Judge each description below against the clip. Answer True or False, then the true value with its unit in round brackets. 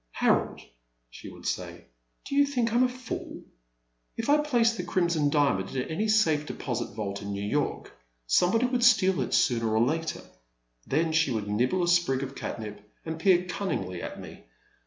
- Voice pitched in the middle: True (160 Hz)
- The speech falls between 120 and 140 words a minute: False (180 wpm)